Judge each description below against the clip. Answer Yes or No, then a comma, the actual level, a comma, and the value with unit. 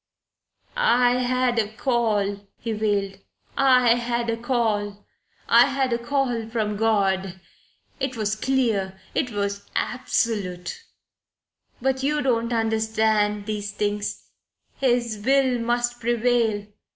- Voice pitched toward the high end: Yes, high, 230 Hz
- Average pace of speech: No, slow, 115 wpm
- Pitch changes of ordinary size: Yes, average, 3.0 semitones